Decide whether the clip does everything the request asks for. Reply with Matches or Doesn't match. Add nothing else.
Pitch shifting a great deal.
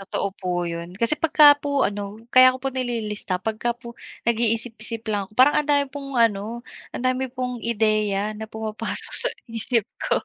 Doesn't match